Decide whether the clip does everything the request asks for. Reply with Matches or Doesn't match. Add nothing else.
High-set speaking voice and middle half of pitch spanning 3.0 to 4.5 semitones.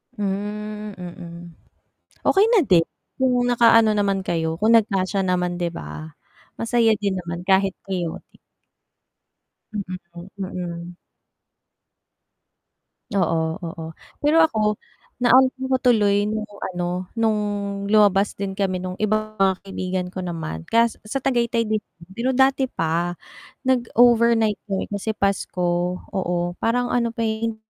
Matches